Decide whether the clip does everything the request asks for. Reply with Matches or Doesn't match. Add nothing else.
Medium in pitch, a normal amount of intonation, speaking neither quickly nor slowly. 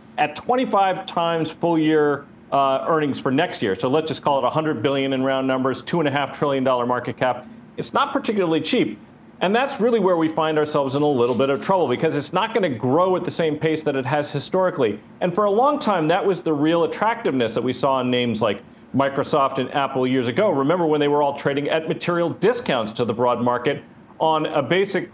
Doesn't match